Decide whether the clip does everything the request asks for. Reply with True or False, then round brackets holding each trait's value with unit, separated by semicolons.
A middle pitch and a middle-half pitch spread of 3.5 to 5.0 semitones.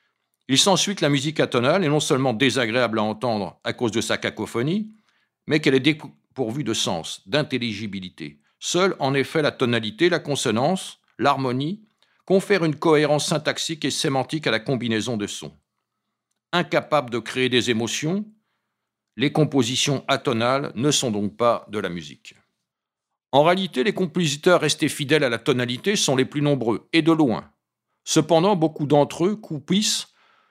False (145 Hz; 5.4 semitones)